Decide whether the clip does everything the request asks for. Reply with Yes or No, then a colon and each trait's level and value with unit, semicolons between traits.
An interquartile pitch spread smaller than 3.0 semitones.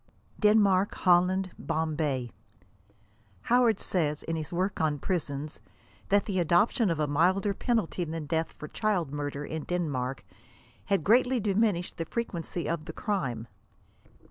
No: average, 4.7 semitones